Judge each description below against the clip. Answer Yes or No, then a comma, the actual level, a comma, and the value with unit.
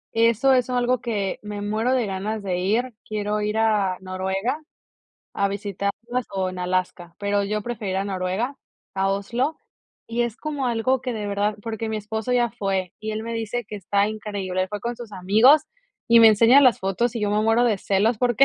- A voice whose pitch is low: No, high, 215 Hz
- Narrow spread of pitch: No, average, 3.1 semitones